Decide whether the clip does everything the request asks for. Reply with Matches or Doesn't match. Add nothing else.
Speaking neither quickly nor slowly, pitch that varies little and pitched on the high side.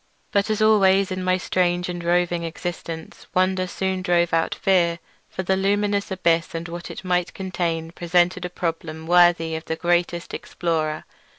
Doesn't match